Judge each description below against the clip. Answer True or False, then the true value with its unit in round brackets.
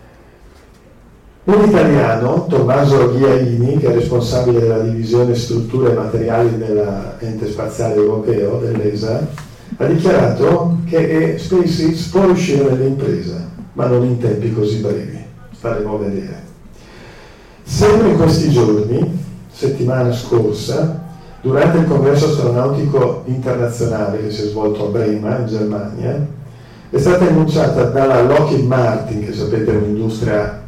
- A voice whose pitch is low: True (120 Hz)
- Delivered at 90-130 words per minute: True (120 wpm)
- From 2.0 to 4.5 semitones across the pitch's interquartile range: False (4.9 semitones)